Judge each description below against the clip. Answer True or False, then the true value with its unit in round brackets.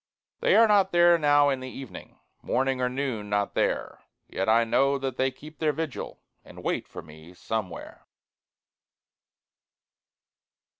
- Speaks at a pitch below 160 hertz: True (135 Hz)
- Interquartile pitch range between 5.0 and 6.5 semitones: True (5.3 semitones)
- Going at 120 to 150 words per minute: True (145 wpm)